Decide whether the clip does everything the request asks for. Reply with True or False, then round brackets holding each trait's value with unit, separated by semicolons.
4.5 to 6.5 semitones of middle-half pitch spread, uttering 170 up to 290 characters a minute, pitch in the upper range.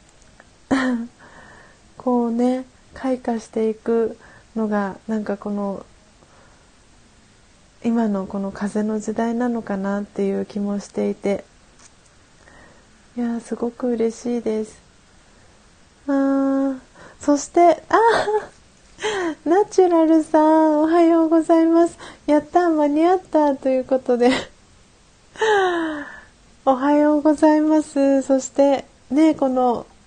True (5.4 semitones; 200 characters per minute; 265 Hz)